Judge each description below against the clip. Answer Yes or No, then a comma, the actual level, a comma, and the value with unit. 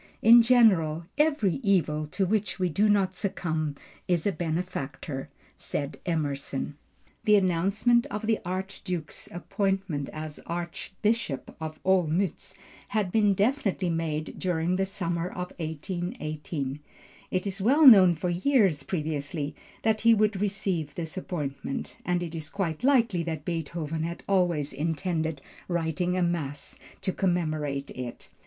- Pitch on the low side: No, medium, 175 Hz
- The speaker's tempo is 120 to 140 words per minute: Yes, slow, 135 wpm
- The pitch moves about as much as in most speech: Yes, average, 4.0 semitones